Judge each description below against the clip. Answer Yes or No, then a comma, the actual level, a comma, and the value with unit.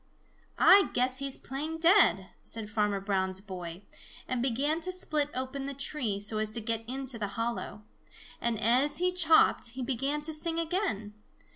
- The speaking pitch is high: Yes, very high, 255 Hz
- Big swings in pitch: Yes, wide, 5.8 semitones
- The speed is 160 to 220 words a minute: Yes, average, 165 wpm